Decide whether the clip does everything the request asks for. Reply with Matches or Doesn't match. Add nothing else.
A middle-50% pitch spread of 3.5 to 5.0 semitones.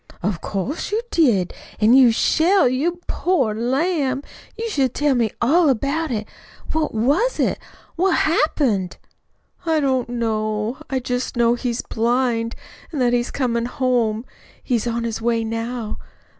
Matches